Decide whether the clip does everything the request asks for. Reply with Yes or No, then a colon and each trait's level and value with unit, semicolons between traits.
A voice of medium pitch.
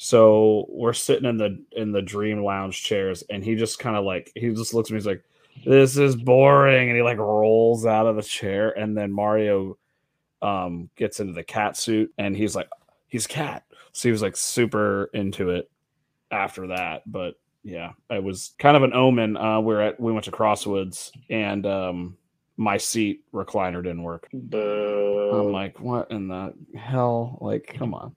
No: low, 105 Hz